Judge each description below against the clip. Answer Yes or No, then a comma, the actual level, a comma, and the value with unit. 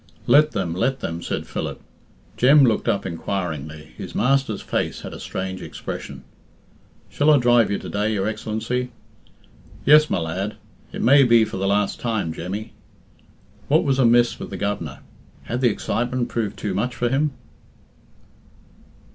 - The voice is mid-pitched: No, low, 110 Hz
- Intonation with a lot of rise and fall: No, average, 4.6 semitones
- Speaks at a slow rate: No, average, 155 wpm